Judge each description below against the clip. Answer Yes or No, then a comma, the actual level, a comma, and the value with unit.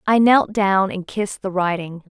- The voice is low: No, high, 195 Hz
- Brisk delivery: No, average, 195 wpm